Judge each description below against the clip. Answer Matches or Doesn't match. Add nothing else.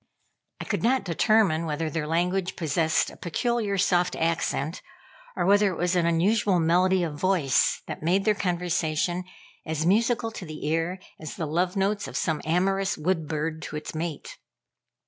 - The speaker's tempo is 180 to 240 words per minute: Doesn't match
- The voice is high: Doesn't match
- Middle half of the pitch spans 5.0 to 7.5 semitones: Doesn't match